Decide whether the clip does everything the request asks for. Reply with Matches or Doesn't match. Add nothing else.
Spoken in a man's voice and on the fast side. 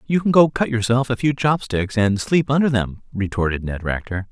Matches